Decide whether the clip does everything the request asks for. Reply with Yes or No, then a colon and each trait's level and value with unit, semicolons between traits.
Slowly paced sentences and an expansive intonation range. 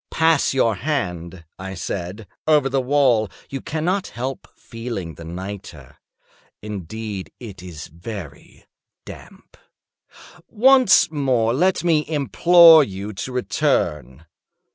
Yes: slow, 110 wpm; wide, 8.0 semitones